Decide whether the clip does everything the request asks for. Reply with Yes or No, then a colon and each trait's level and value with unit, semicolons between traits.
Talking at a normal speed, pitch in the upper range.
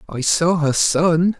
No: average, 170 wpm; medium, 165 Hz